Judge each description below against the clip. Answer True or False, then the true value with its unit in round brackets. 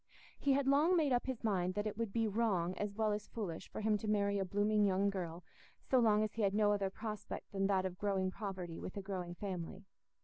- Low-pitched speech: False (205 Hz)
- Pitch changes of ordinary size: False (2.3 semitones)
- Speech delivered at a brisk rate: True (240 wpm)